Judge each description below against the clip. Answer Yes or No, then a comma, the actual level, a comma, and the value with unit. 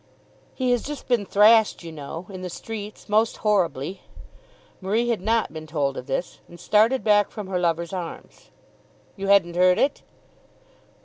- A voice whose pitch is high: Yes, high, 195 Hz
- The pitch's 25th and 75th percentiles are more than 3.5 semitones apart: Yes, average, 4.3 semitones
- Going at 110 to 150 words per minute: No, average, 165 wpm